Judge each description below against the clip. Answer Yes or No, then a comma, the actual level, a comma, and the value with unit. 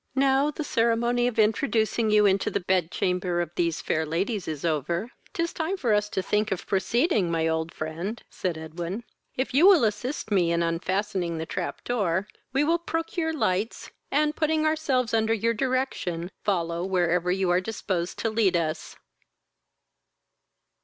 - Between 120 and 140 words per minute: No, average, 165 wpm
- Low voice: No, high, 205 Hz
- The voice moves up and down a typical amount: No, wide, 6.1 semitones